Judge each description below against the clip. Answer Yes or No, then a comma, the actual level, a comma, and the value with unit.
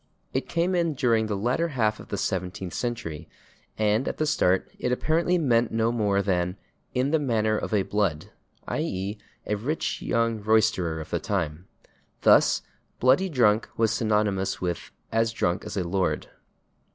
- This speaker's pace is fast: No, average, 165 wpm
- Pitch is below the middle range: Yes, low, 110 Hz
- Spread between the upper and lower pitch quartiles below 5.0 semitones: Yes, average, 4.3 semitones